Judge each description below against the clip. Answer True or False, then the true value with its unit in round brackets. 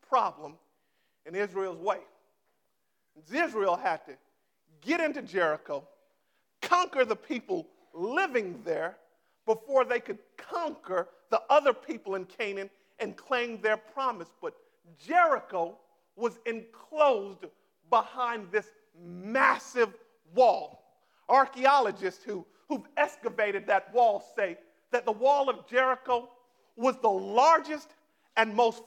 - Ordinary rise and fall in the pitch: False (6.2 semitones)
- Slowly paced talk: True (110 wpm)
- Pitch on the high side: True (245 Hz)